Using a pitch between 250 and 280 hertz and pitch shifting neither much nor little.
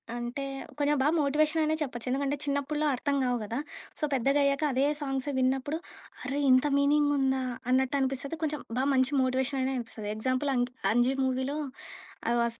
No: very high, 270 Hz; narrow, 2.0 semitones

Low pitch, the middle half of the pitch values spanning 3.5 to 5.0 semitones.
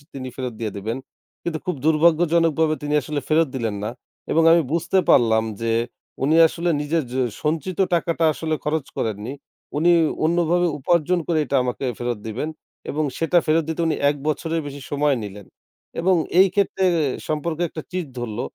No: medium, 155 Hz; average, 4.1 semitones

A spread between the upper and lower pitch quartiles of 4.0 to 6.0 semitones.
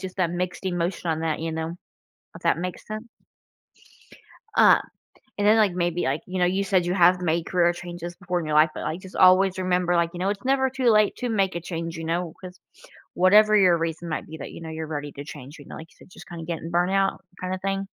No: narrow, 2.4 semitones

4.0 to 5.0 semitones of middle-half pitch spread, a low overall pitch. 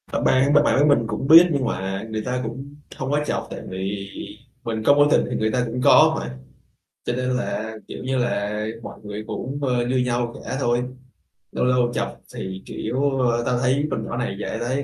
No: average, 3.2 semitones; low, 125 Hz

